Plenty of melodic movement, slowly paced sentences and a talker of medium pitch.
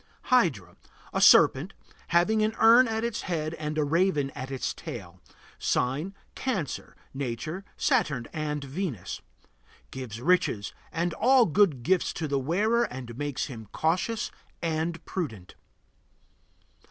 Yes: wide, 6.6 semitones; slow, 130 wpm; medium, 155 Hz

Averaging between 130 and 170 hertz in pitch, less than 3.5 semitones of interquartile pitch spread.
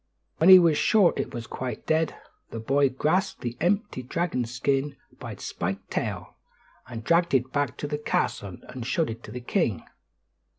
No: low, 135 Hz; wide, 5.6 semitones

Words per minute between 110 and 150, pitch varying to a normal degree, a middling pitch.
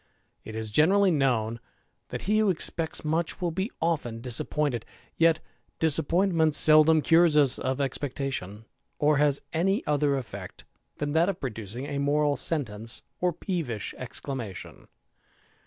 Yes: slow, 135 wpm; average, 4.7 semitones; medium, 145 Hz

